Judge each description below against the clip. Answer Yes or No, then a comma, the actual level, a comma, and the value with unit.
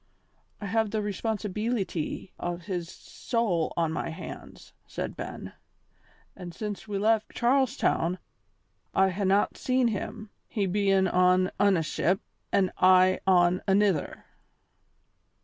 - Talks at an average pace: No, slow, 125 wpm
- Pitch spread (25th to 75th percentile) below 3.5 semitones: Yes, average, 2.8 semitones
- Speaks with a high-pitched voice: Yes, high, 195 Hz